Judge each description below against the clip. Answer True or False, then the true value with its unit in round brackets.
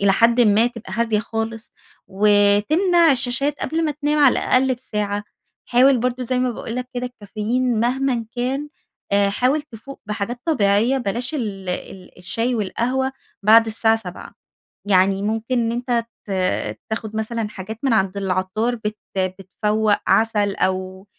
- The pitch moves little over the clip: False (3.6 semitones)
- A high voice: True (225 Hz)